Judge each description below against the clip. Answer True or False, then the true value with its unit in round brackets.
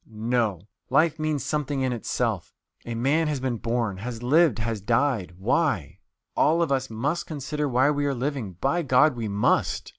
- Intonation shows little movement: False (4.5 semitones)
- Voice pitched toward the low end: True (130 Hz)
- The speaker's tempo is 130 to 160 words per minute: False (175 wpm)